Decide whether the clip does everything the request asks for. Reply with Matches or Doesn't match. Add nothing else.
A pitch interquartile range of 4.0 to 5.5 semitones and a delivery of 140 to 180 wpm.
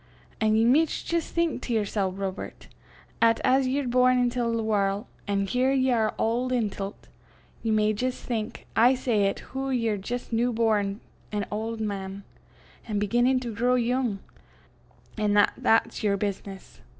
Doesn't match